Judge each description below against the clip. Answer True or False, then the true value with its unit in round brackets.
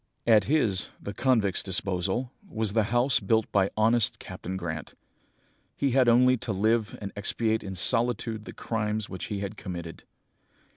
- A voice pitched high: False (110 Hz)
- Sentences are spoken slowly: False (155 wpm)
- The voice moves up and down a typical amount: True (3.3 semitones)